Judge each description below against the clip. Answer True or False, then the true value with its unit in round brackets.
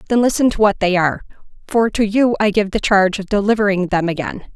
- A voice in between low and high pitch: False (205 Hz)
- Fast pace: True (225 wpm)